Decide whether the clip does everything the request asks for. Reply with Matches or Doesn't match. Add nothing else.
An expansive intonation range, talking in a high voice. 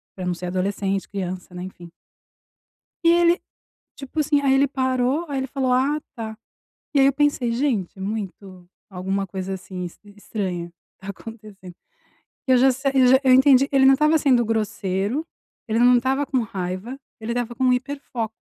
Matches